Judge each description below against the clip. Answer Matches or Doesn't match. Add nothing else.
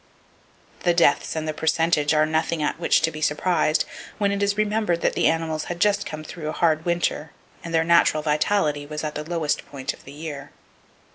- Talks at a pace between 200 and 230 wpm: Matches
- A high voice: Doesn't match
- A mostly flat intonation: Matches